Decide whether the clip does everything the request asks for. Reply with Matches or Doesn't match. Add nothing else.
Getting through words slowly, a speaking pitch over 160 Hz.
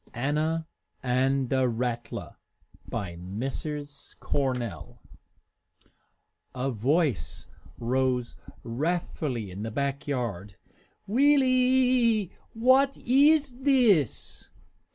Doesn't match